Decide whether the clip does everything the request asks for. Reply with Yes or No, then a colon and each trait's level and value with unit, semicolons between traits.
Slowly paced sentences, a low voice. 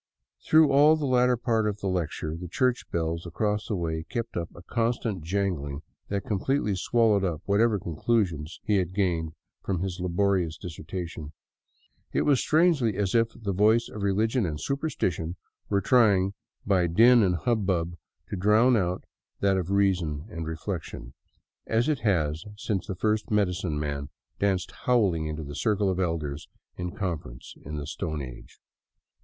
No: average, 160 wpm; very low, 95 Hz